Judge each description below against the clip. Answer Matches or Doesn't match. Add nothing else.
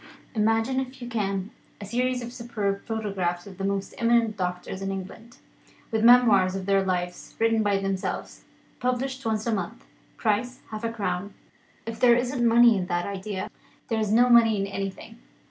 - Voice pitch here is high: Matches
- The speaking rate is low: Doesn't match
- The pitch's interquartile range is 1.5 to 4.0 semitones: Matches